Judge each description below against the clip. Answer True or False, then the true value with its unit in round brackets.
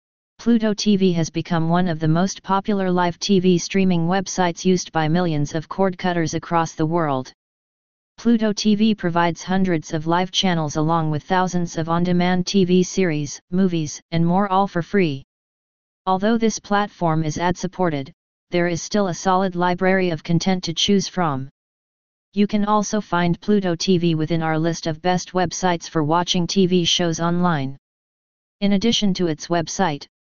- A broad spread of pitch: False (2.4 semitones)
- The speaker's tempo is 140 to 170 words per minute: True (160 wpm)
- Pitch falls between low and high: True (180 Hz)